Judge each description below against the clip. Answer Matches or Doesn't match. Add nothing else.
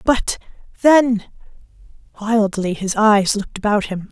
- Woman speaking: Matches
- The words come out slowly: Matches